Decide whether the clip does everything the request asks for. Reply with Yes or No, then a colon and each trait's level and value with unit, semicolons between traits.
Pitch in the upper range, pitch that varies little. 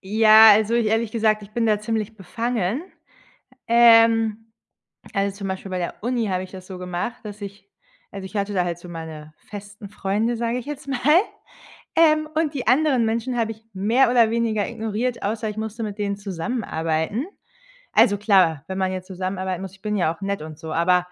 No: high, 210 Hz; average, 3.4 semitones